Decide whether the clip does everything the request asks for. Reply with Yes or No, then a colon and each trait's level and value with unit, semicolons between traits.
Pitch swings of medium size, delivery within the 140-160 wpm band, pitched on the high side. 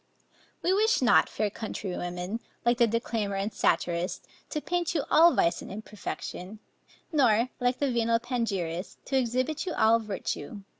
Yes: average, 4.5 semitones; average, 150 wpm; high, 230 Hz